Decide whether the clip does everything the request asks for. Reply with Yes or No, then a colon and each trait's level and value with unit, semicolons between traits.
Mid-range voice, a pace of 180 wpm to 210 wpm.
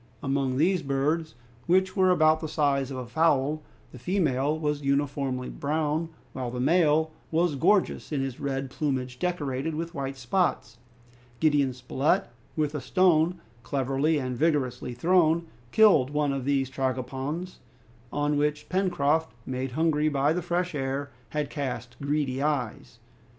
No: medium, 145 Hz; average, 145 wpm